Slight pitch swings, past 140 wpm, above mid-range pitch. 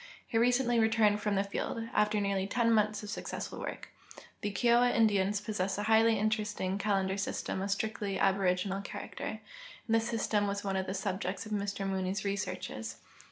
Yes: narrow, 2.2 semitones; average, 170 wpm; high, 205 Hz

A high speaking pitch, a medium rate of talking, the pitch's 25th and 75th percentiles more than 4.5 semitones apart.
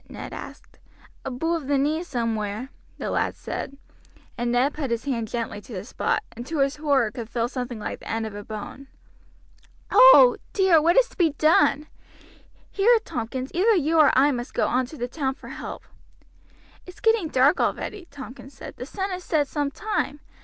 Yes: very high, 275 Hz; average, 190 wpm; average, 5.2 semitones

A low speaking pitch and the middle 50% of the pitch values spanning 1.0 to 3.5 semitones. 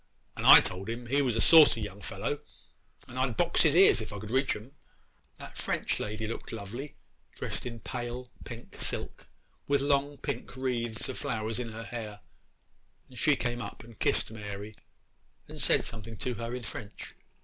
Yes: low, 115 Hz; average, 3.0 semitones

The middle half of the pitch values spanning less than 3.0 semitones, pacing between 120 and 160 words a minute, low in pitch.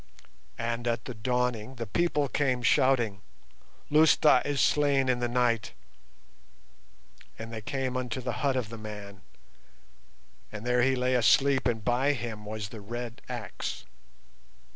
Yes: narrow, 2.6 semitones; average, 140 wpm; low, 120 Hz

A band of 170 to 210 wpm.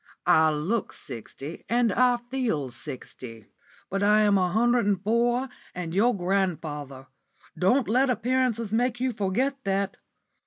No: average, 140 wpm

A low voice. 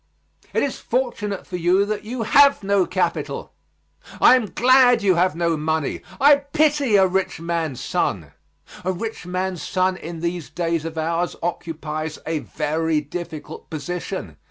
No: medium, 180 Hz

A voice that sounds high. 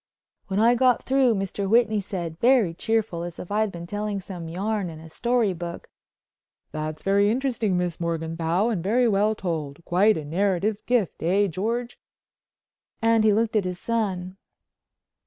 Yes: high, 200 Hz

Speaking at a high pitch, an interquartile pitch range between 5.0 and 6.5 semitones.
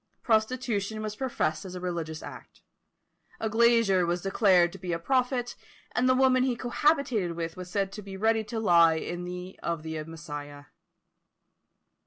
Yes: high, 195 Hz; wide, 5.5 semitones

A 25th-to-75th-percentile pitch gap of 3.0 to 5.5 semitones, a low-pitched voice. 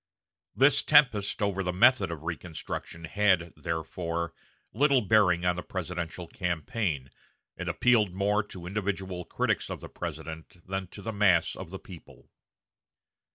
Yes: average, 3.5 semitones; very low, 95 Hz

